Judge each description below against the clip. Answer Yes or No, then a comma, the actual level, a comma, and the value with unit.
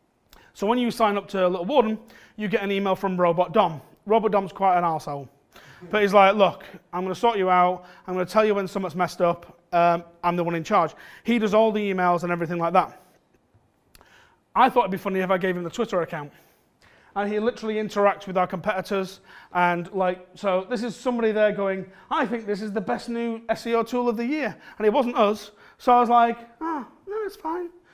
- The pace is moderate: No, fast, 230 wpm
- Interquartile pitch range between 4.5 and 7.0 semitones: No, average, 4.1 semitones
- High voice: Yes, high, 200 Hz